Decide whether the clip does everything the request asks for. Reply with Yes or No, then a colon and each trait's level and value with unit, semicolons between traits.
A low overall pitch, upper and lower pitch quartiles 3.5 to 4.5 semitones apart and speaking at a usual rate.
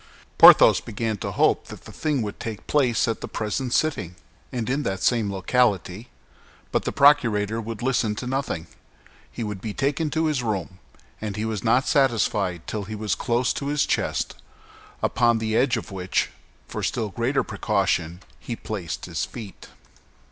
Yes: low, 110 Hz; average, 3.8 semitones; average, 170 wpm